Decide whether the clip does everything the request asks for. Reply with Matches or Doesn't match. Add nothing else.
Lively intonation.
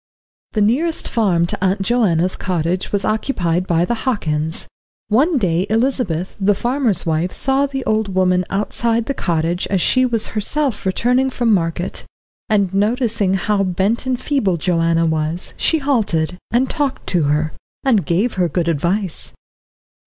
Matches